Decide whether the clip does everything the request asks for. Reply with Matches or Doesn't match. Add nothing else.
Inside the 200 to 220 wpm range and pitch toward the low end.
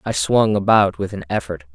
Matches